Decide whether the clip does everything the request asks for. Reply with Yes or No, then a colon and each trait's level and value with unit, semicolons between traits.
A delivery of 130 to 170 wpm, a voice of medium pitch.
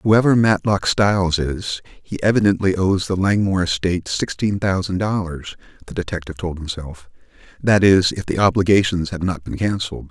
No: average, 155 wpm; very low, 90 Hz